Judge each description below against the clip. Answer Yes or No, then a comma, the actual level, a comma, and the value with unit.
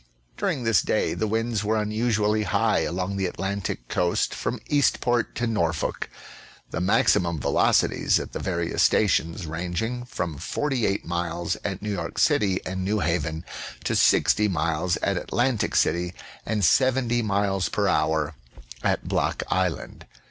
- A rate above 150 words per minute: No, average, 140 wpm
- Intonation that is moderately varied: Yes, average, 4.2 semitones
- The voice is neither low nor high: No, very low, 95 Hz